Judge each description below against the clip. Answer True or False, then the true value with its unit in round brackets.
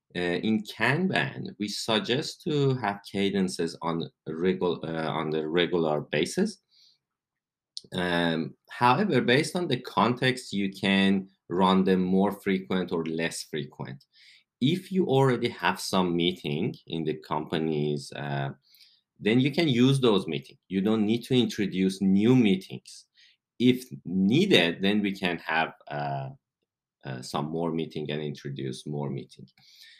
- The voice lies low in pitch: True (95 Hz)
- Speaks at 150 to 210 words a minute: False (135 wpm)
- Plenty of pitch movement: True (7.4 semitones)